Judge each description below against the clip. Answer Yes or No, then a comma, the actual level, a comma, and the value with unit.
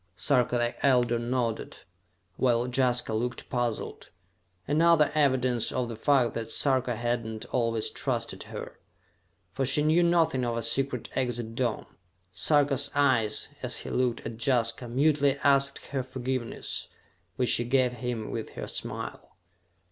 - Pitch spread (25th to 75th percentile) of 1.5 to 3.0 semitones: Yes, narrow, 2.5 semitones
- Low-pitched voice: Yes, low, 125 Hz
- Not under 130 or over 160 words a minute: Yes, average, 140 wpm